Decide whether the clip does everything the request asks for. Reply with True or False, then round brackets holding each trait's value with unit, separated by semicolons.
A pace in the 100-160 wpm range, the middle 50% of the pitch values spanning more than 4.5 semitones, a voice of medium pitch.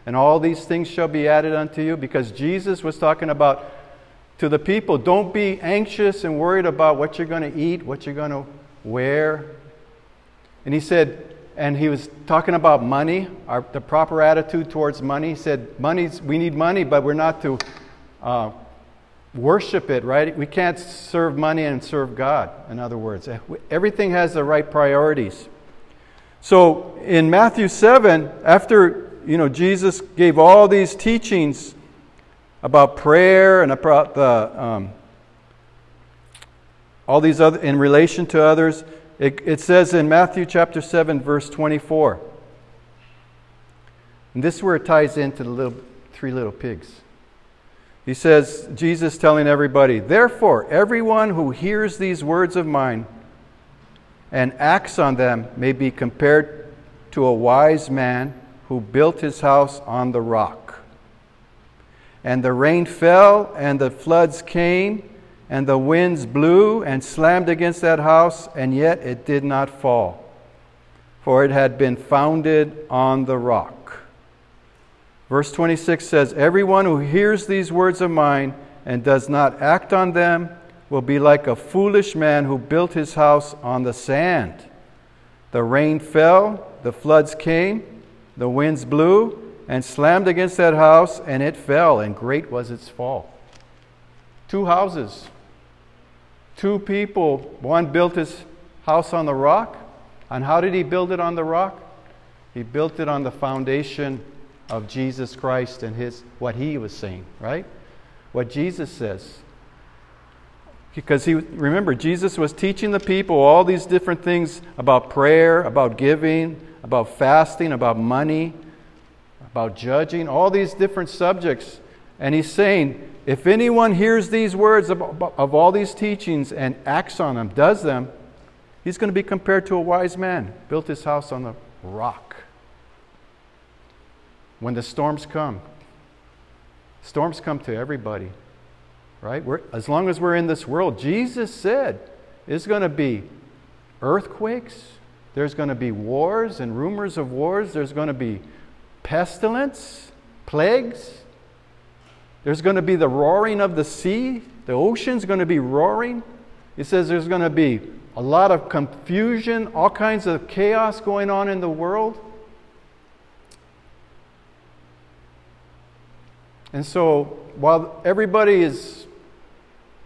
True (145 wpm; 5.6 semitones; 150 Hz)